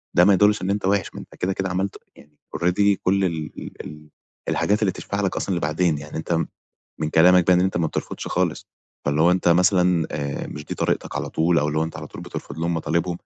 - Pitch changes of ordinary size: Yes, average, 3.1 semitones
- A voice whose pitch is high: No, very low, 90 Hz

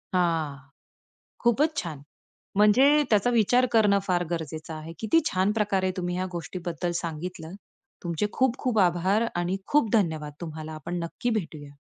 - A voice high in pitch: No, medium, 180 Hz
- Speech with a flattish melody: No, average, 4.4 semitones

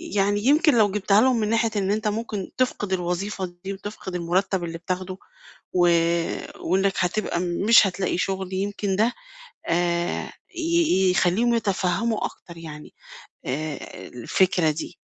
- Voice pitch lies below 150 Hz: No, high, 190 Hz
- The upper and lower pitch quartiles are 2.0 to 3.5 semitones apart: Yes, average, 3.1 semitones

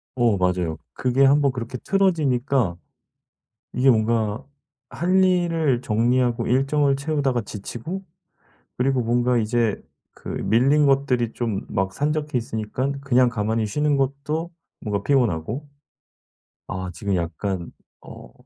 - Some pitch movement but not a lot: Yes, average, 4.4 semitones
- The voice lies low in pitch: Yes, low, 125 Hz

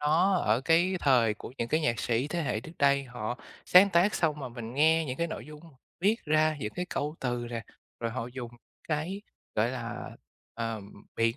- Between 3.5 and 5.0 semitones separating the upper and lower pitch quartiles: No, wide, 5.5 semitones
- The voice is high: No, medium, 140 Hz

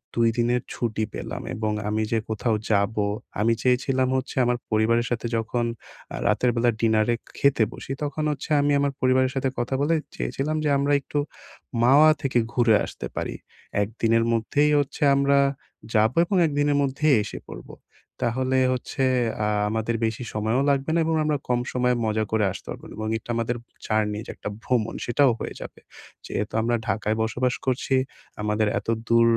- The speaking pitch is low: Yes, low, 120 Hz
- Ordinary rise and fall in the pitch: Yes, average, 3.5 semitones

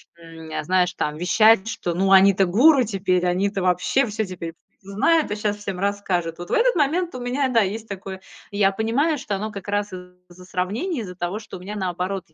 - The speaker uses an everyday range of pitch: Yes, average, 3.5 semitones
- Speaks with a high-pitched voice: Yes, high, 195 Hz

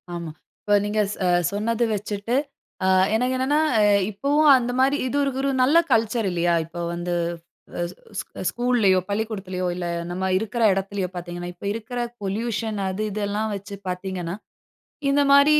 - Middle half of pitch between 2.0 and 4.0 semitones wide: No, average, 4.6 semitones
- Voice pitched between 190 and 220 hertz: Yes, high, 210 Hz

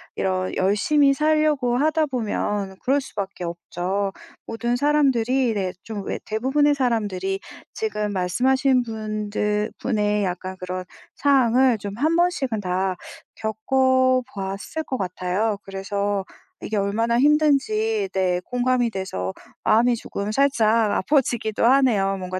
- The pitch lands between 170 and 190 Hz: No, high, 225 Hz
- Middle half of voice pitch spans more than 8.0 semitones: No, average, 5.3 semitones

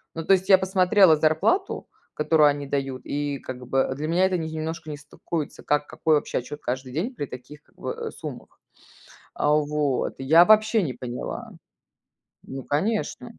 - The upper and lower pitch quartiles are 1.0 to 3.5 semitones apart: No, average, 4.1 semitones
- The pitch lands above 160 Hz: No, medium, 150 Hz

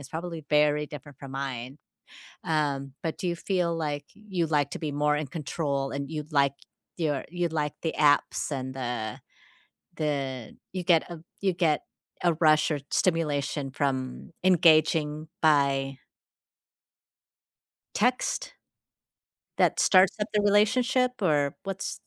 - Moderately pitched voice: Yes, medium, 150 Hz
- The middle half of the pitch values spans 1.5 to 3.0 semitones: No, average, 3.5 semitones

